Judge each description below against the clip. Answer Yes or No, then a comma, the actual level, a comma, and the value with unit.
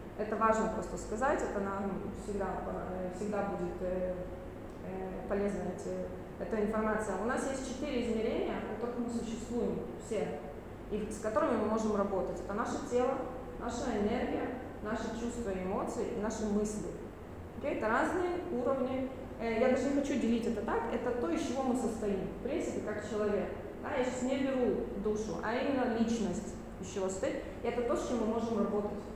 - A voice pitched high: Yes, high, 220 Hz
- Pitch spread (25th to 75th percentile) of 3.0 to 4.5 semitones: Yes, average, 3.8 semitones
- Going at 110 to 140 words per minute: No, average, 155 wpm